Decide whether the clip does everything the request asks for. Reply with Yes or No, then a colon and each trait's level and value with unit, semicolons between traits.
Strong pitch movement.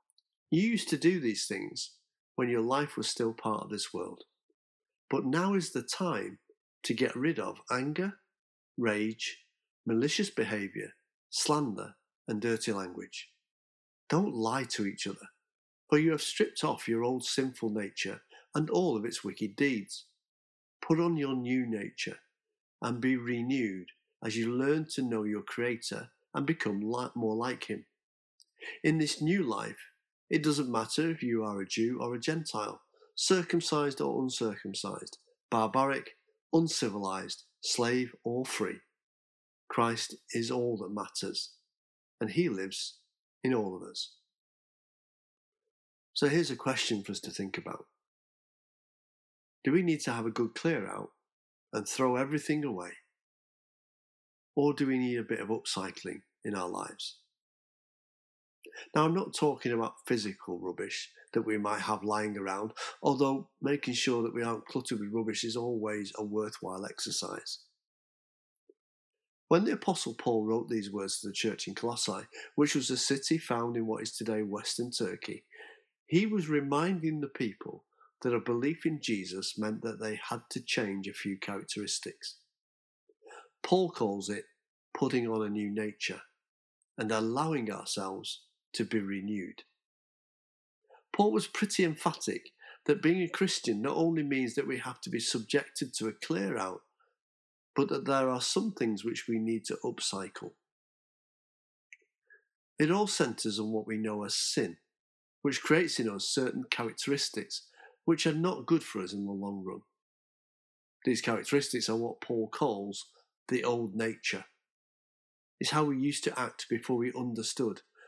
Yes: wide, 6.0 semitones